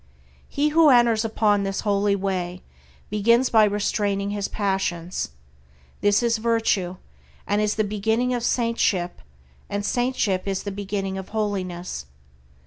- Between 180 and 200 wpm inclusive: No, slow, 135 wpm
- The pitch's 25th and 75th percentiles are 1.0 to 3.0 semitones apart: Yes, narrow, 2.6 semitones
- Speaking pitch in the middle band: No, high, 205 Hz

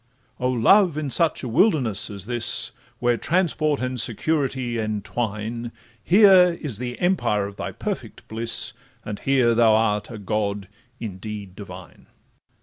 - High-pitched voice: No, low, 115 Hz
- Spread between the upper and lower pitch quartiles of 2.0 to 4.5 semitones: No, average, 4.9 semitones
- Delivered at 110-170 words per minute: Yes, average, 140 wpm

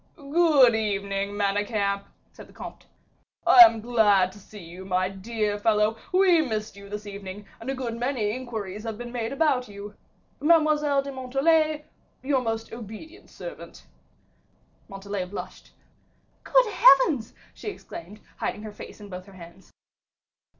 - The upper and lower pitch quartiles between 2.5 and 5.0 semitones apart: No, wide, 5.5 semitones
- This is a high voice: Yes, high, 220 Hz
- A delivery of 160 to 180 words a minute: No, average, 145 wpm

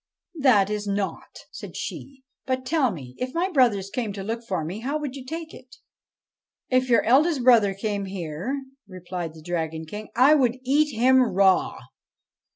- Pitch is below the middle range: No, high, 230 Hz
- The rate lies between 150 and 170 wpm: No, average, 195 wpm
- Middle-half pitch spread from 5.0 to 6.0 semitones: Yes, average, 5.3 semitones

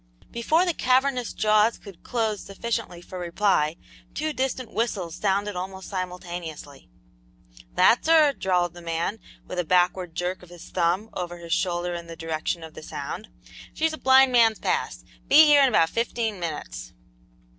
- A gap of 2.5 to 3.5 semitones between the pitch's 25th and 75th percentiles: No, average, 5.3 semitones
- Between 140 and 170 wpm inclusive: Yes, average, 160 wpm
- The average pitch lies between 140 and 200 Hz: Yes, high, 190 Hz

